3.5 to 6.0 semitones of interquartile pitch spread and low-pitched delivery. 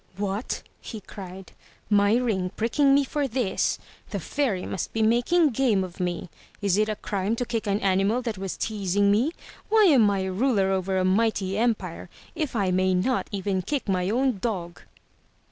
No: average, 4.1 semitones; high, 205 Hz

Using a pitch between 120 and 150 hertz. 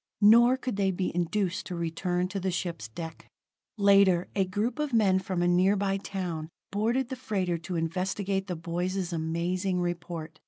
No: medium, 185 Hz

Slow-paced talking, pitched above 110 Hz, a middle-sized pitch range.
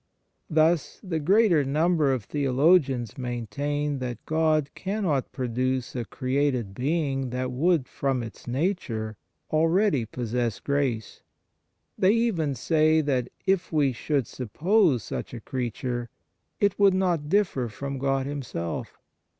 Yes: slow, 125 wpm; medium, 140 Hz; average, 4.5 semitones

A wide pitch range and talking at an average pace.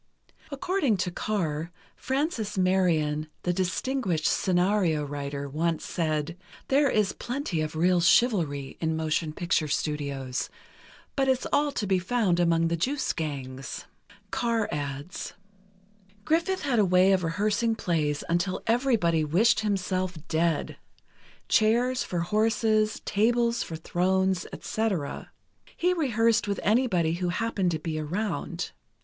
No: wide, 5.8 semitones; slow, 120 wpm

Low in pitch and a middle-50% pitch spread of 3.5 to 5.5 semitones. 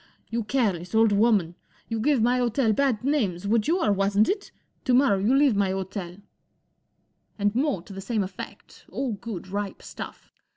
No: high, 215 Hz; average, 4.2 semitones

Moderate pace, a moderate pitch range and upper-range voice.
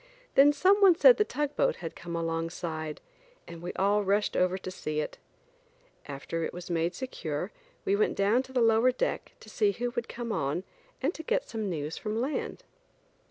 No: average, 190 wpm; wide, 8.1 semitones; high, 210 Hz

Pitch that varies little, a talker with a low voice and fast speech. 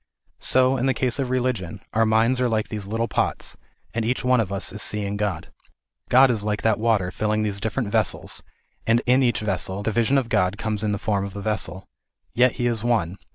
No: average, 3.0 semitones; low, 110 Hz; fast, 220 wpm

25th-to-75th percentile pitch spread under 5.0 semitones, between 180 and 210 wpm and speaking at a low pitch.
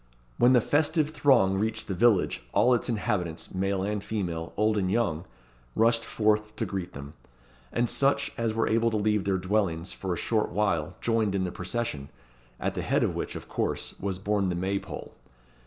Yes: average, 3.5 semitones; average, 190 wpm; low, 105 Hz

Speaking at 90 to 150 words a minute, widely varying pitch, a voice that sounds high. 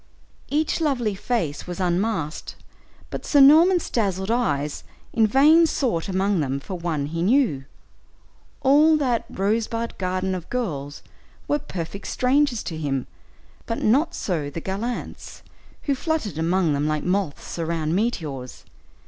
Yes: slow, 135 wpm; wide, 7.4 semitones; high, 195 Hz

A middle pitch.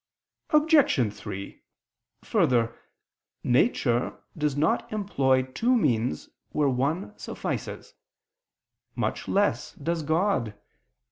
Yes: medium, 145 Hz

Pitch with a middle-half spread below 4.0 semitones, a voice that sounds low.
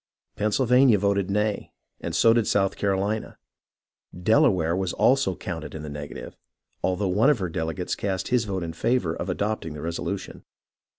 Yes: average, 3.6 semitones; very low, 95 Hz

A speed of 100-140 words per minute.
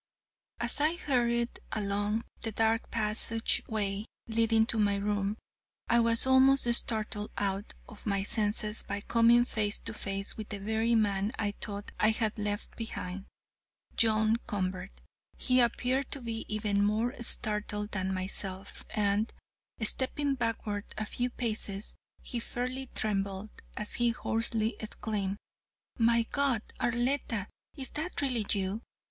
Yes: slow, 135 wpm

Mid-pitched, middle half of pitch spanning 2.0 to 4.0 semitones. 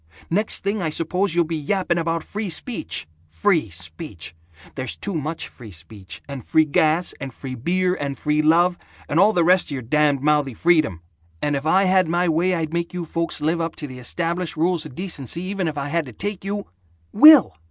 No: medium, 165 Hz; average, 4.5 semitones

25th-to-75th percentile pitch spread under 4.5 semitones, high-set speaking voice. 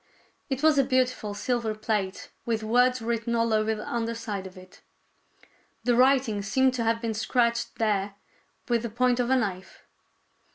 Yes: narrow, 2.6 semitones; high, 230 Hz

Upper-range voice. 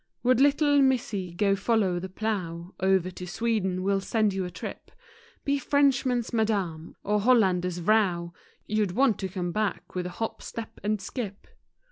Yes: high, 200 Hz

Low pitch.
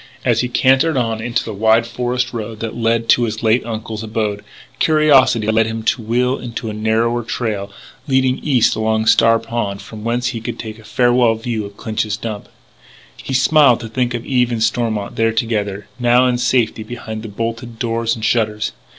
Yes: low, 115 Hz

